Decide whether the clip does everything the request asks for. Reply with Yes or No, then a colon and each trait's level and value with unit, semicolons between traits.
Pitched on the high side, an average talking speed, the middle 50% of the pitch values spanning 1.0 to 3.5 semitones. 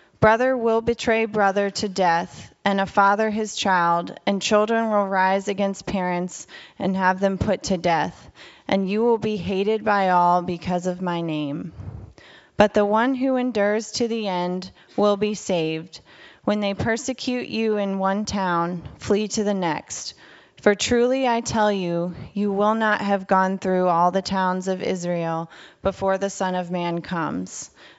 Yes: high, 195 Hz; average, 165 wpm; average, 2.9 semitones